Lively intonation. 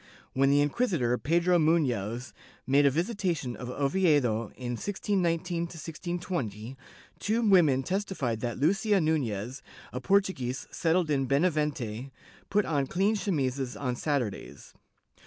Yes: wide, 6.1 semitones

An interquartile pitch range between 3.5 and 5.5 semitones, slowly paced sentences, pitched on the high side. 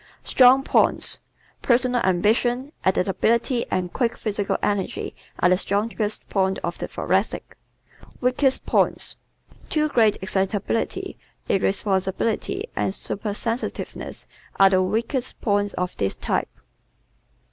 Yes: average, 4.0 semitones; slow, 115 wpm; high, 210 Hz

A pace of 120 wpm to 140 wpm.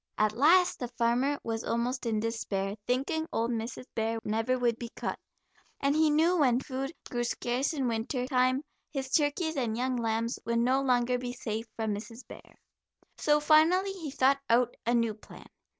No: average, 180 wpm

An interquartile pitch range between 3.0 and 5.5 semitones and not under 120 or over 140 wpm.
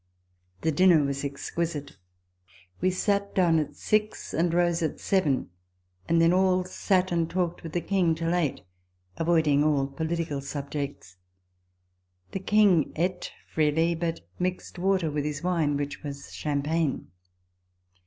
Yes: average, 3.5 semitones; slow, 135 wpm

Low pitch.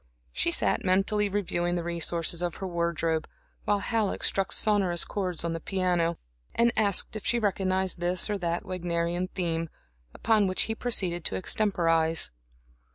No: medium, 180 Hz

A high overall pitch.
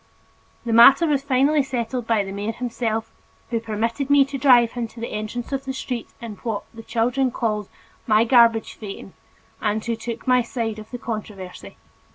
Yes: high, 230 Hz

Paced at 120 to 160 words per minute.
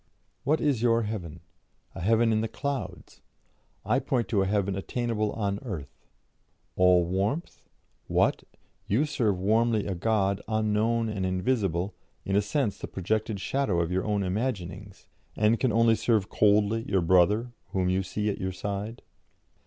Yes: average, 155 wpm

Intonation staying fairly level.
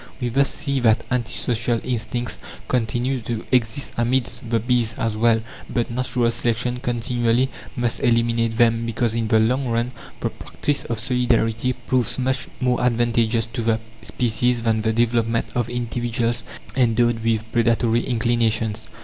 Yes: narrow, 1.3 semitones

